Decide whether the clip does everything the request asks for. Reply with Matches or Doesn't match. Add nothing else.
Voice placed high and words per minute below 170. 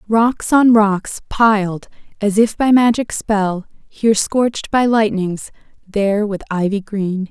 Matches